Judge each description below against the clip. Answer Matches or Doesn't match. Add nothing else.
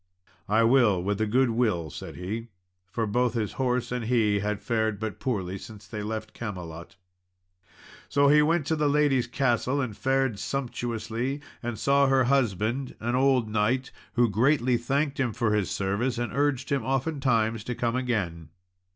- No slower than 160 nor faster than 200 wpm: Matches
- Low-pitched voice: Matches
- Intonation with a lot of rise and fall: Doesn't match